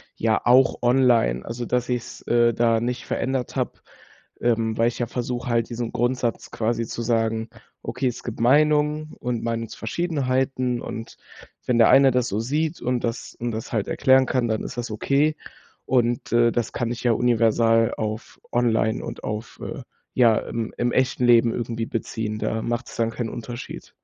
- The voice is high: No, low, 120 Hz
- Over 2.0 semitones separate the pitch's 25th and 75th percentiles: No, narrow, 1.7 semitones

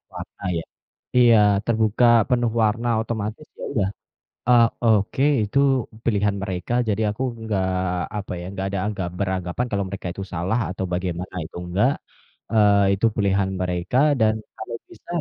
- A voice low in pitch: Yes, low, 105 Hz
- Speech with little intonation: No, average, 3.0 semitones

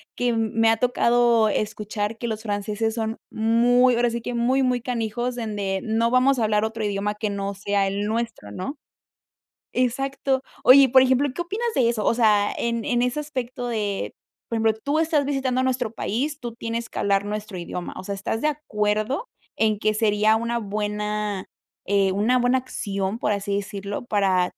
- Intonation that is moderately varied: Yes, average, 3.1 semitones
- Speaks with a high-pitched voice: Yes, high, 225 Hz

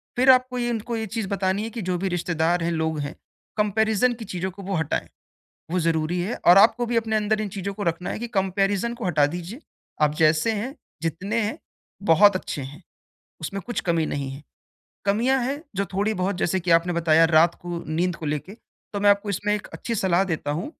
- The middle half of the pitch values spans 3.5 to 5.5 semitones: Yes, average, 4.4 semitones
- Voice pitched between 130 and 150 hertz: No, high, 190 Hz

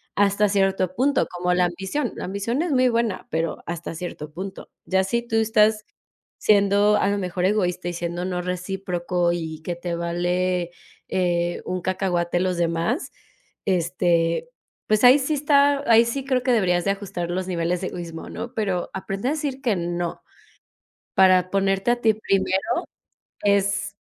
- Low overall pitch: No, high, 190 Hz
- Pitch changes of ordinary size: Yes, average, 3.4 semitones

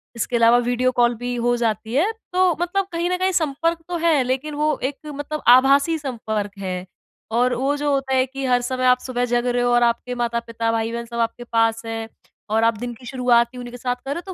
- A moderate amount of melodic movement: Yes, average, 3.2 semitones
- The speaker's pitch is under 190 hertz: No, high, 245 Hz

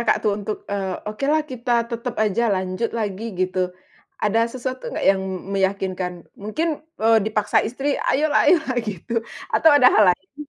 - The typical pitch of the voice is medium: No, high, 220 Hz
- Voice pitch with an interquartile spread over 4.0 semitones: Yes, average, 4.6 semitones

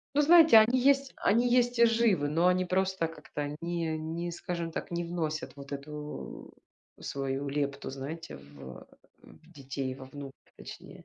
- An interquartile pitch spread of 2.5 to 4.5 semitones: No, average, 5.2 semitones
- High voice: No, medium, 165 Hz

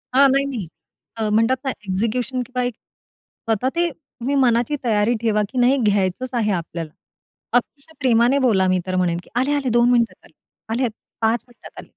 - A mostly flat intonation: No, average, 3.5 semitones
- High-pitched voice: Yes, high, 240 Hz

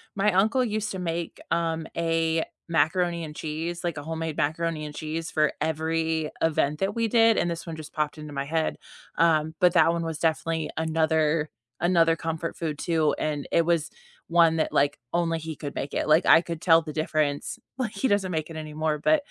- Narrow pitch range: Yes, narrow, 1.5 semitones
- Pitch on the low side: No, medium, 165 Hz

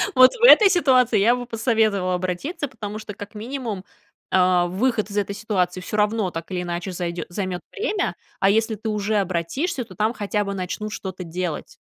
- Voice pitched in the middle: No, high, 205 Hz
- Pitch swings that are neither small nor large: Yes, average, 4.1 semitones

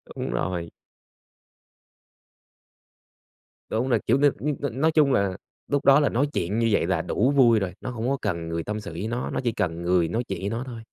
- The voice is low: Yes, low, 110 Hz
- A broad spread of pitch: Yes, wide, 6.0 semitones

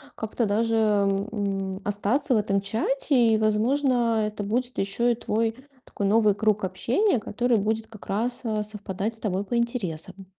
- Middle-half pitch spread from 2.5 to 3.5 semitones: Yes, average, 2.8 semitones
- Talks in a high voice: Yes, high, 215 Hz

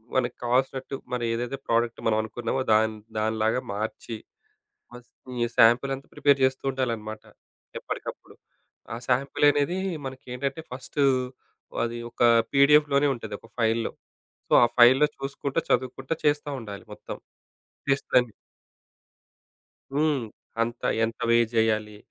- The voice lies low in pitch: Yes, low, 125 Hz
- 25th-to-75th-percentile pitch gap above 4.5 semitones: No, average, 3.2 semitones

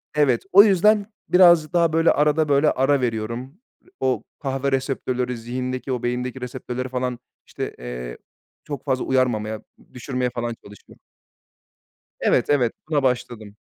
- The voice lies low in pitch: Yes, low, 130 Hz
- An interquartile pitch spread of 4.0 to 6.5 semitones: No, average, 3.2 semitones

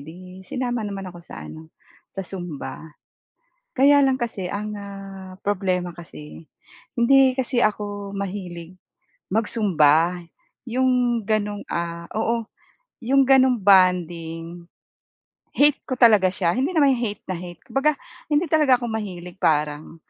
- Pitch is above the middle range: Yes, high, 200 Hz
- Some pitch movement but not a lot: No, wide, 5.7 semitones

